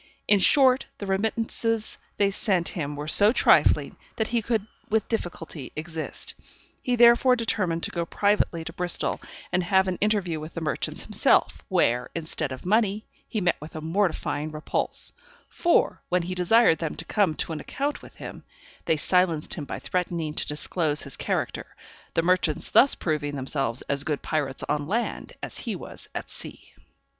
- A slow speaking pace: No, average, 170 wpm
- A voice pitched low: No, medium, 175 Hz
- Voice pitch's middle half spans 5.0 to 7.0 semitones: Yes, average, 5.3 semitones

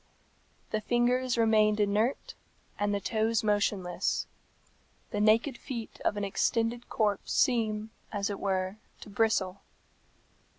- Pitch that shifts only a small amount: Yes, narrow, 2.0 semitones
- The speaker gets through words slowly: Yes, slow, 120 wpm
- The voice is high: Yes, high, 215 Hz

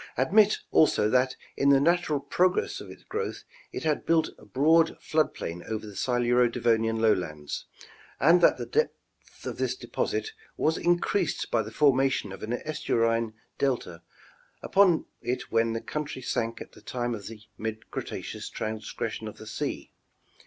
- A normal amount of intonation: No, wide, 5.8 semitones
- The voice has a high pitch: No, low, 125 Hz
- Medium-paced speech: Yes, average, 160 wpm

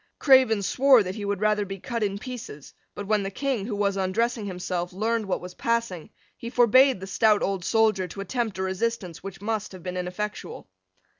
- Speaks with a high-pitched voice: Yes, high, 205 Hz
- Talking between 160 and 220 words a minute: Yes, average, 200 wpm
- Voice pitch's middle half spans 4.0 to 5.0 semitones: No, average, 3.5 semitones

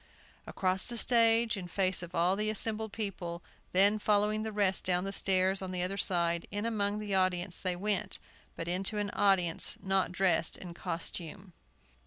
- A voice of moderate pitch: No, high, 195 Hz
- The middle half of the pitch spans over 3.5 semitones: No, narrow, 2.5 semitones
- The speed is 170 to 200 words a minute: Yes, average, 175 wpm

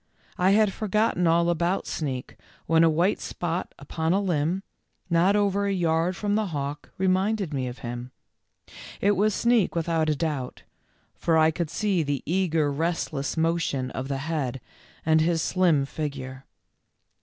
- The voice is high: No, medium, 165 Hz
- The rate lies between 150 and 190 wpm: Yes, average, 160 wpm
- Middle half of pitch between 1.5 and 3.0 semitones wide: No, average, 4.2 semitones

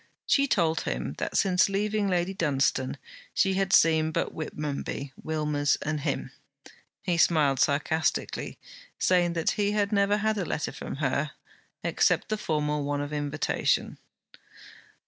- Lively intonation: No, average, 4.9 semitones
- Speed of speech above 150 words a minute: No, slow, 135 wpm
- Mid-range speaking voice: Yes, medium, 160 Hz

